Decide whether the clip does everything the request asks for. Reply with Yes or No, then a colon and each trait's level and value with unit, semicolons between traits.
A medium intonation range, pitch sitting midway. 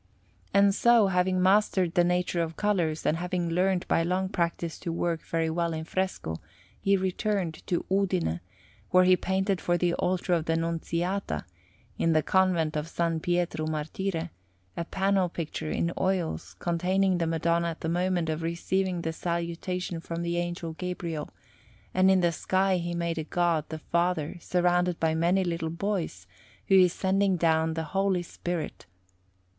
No: narrow, 2.1 semitones; medium, 175 Hz